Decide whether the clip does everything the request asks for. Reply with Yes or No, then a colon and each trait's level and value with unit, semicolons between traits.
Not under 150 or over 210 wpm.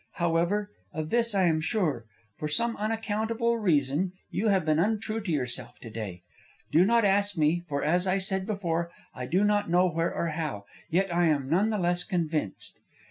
Yes: average, 190 wpm